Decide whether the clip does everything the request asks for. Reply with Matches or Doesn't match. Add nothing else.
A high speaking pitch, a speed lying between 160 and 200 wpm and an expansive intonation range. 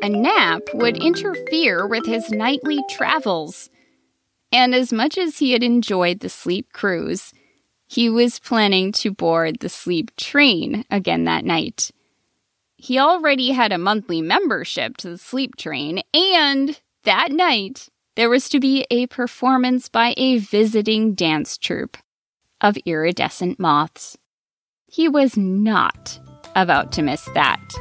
Doesn't match